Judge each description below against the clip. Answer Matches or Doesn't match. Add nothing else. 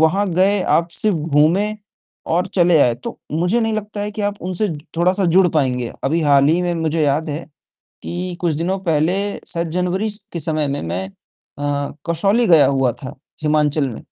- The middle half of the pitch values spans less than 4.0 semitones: Doesn't match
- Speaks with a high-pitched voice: Doesn't match